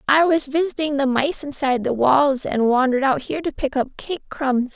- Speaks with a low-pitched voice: No, very high, 275 Hz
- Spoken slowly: No, fast, 215 wpm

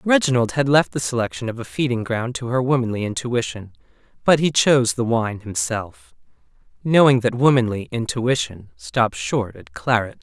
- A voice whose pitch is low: Yes, low, 120 Hz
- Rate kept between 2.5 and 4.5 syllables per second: No, 5.0 syllables/s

